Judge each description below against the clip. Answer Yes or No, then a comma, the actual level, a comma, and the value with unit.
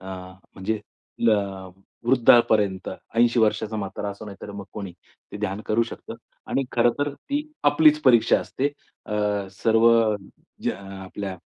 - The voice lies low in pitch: Yes, low, 110 Hz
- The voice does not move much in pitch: No, average, 3.1 semitones